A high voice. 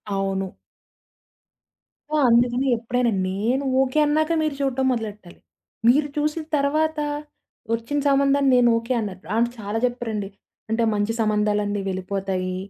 Yes: high, 235 Hz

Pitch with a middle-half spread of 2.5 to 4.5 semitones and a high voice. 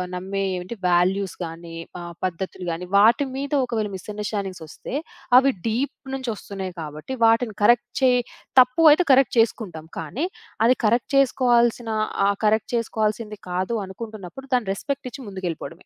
No: average, 4.9 semitones; high, 215 Hz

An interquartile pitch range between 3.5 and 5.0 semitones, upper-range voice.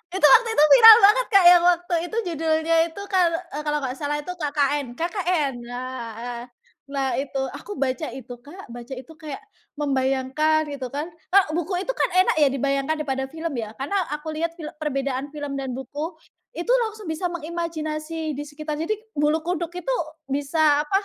Yes: average, 3.9 semitones; very high, 305 Hz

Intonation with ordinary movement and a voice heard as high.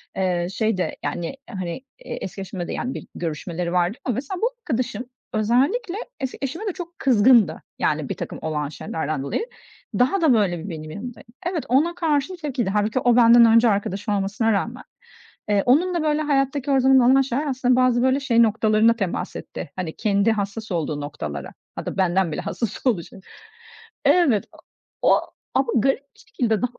No: wide, 5.9 semitones; high, 230 Hz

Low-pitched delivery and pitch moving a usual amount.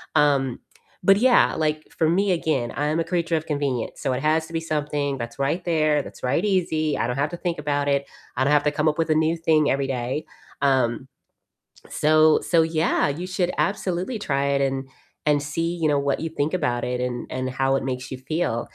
No: medium, 150 Hz; average, 3.2 semitones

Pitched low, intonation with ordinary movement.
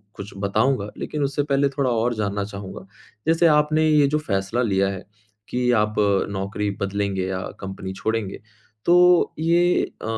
No: low, 110 Hz; wide, 6.8 semitones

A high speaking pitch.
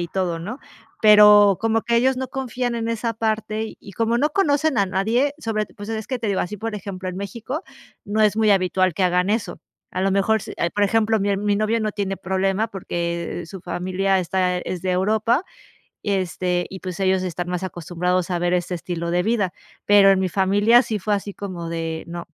Yes: high, 200 Hz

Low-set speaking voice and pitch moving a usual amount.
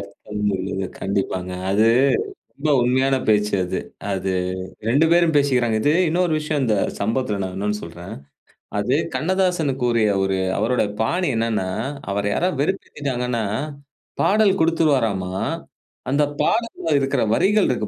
No: low, 125 Hz; wide, 7.1 semitones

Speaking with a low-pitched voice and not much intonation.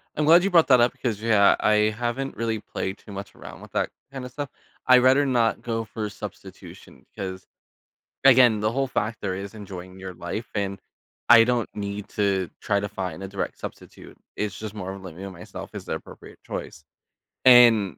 No: low, 105 Hz; average, 3.9 semitones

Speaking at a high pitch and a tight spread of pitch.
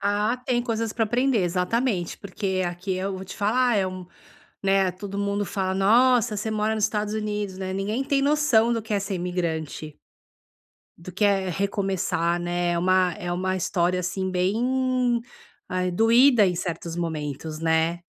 No: high, 195 Hz; average, 3.5 semitones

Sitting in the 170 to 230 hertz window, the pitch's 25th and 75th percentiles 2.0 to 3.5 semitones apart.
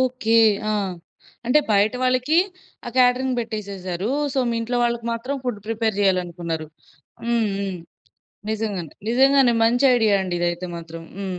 No: high, 220 Hz; average, 4.8 semitones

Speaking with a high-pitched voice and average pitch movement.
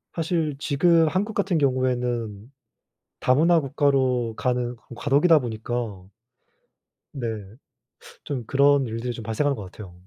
No: low, 130 Hz; average, 4.1 semitones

